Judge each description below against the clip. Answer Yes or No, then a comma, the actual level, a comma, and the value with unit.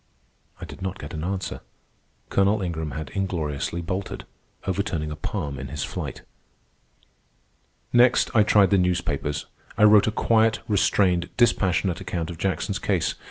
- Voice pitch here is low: Yes, very low, 95 Hz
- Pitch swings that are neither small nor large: Yes, average, 3.7 semitones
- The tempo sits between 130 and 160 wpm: Yes, average, 145 wpm